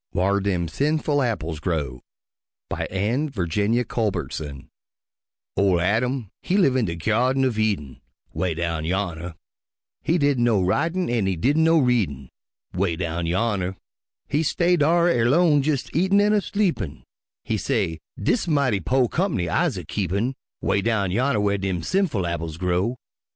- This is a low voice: Yes, low, 105 Hz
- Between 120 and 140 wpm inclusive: No, average, 150 wpm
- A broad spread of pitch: Yes, wide, 8.0 semitones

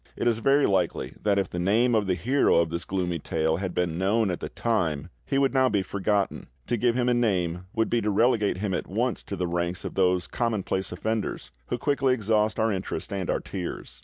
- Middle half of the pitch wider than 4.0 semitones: Yes, average, 4.4 semitones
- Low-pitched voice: Yes, low, 100 Hz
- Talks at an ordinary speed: No, fast, 225 wpm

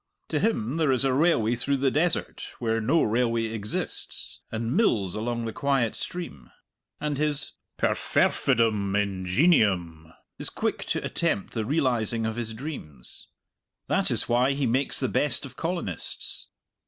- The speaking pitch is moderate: No, low, 120 Hz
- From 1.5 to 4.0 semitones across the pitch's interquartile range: No, average, 4.6 semitones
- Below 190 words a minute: Yes, average, 145 wpm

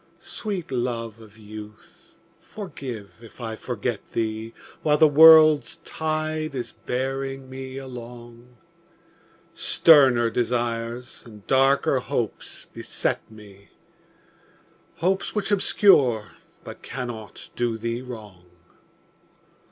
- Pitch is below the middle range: Yes, low, 125 Hz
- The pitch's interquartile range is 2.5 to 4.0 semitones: Yes, average, 3.6 semitones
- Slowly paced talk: Yes, slow, 95 wpm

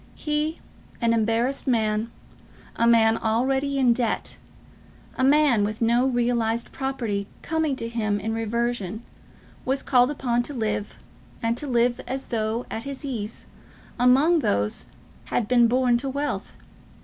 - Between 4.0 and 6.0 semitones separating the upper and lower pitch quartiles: No, average, 3.0 semitones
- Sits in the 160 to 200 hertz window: No, high, 240 Hz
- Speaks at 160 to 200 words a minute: No, average, 145 wpm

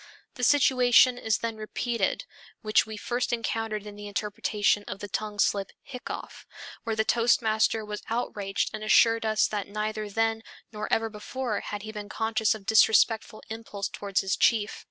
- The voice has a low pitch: No, high, 215 Hz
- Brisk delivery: No, average, 165 wpm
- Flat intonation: Yes, narrow, 1.6 semitones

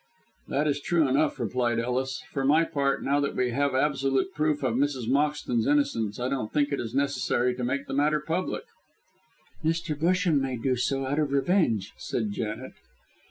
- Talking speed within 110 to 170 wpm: No, average, 180 wpm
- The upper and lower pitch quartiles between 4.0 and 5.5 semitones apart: No, average, 2.9 semitones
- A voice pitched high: No, medium, 140 Hz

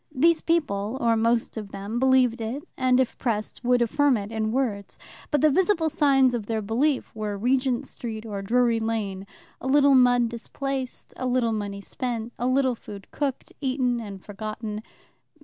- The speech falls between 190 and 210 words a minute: No, average, 170 wpm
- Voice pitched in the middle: No, high, 240 Hz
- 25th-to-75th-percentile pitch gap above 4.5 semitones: No, average, 3.2 semitones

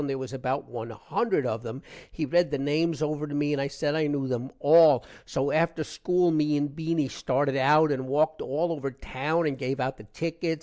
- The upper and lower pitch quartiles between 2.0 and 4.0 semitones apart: Yes, average, 2.9 semitones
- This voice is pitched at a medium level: Yes, medium, 145 Hz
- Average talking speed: No, fast, 220 wpm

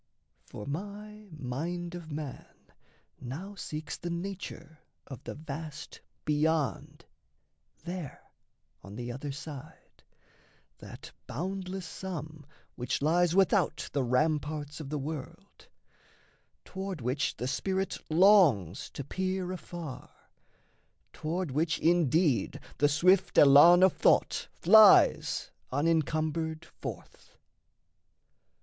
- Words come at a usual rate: No, slow, 100 wpm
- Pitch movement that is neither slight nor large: Yes, average, 4.0 semitones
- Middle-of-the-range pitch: Yes, medium, 160 Hz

